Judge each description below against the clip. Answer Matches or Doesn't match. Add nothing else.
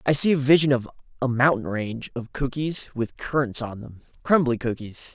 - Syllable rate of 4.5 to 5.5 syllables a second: Matches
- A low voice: Matches